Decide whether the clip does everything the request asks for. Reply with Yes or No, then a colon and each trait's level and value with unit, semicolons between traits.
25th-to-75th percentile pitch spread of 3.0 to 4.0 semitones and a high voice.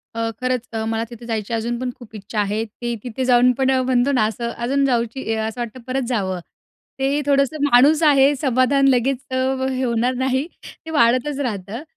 No: narrow, 2.6 semitones; very high, 250 Hz